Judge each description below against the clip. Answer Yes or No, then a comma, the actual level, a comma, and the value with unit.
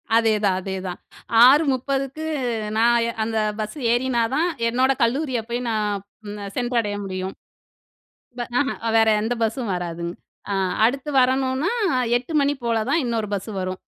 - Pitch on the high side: Yes, high, 235 Hz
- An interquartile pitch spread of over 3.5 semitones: Yes, average, 3.9 semitones